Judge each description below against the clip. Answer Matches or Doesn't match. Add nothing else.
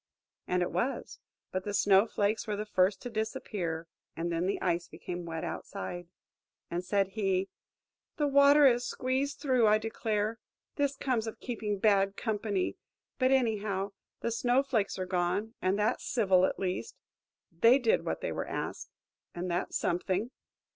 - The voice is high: Matches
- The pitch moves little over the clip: Doesn't match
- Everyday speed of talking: Matches